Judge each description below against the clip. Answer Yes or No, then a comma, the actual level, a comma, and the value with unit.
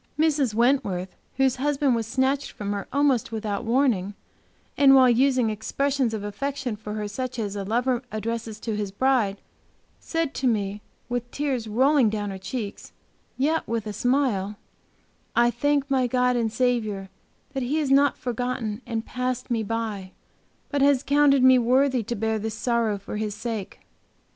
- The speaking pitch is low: No, high, 240 Hz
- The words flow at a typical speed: Yes, average, 165 wpm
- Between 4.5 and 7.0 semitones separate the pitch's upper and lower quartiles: No, average, 3.9 semitones